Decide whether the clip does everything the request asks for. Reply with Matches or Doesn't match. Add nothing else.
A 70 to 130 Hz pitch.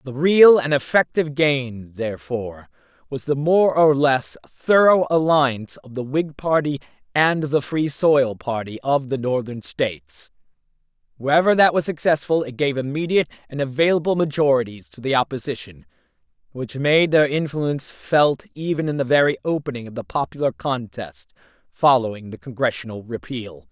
Doesn't match